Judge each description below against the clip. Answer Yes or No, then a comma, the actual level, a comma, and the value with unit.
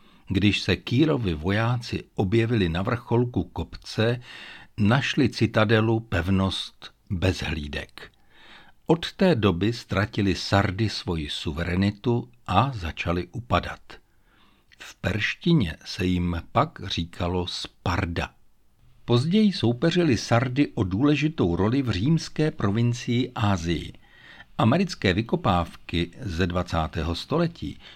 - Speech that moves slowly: Yes, slow, 95 wpm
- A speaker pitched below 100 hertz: No, low, 105 Hz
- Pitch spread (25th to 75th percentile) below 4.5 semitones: No, average, 5.2 semitones